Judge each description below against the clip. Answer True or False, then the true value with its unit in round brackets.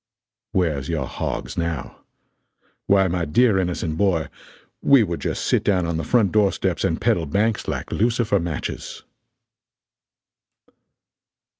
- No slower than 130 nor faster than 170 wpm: True (135 wpm)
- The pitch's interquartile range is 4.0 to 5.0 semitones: True (4.4 semitones)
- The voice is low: True (90 Hz)